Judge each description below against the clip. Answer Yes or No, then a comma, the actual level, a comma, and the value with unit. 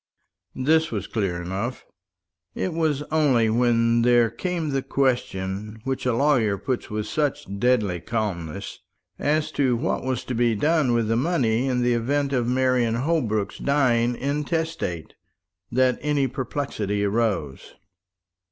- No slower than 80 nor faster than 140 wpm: Yes, slow, 135 wpm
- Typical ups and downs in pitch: Yes, average, 4.1 semitones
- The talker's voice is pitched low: Yes, low, 125 Hz